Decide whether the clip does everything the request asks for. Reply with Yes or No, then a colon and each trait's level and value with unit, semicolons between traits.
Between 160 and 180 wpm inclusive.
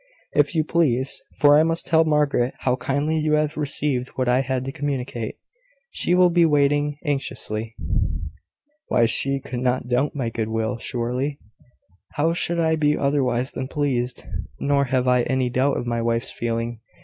Yes: average, 170 wpm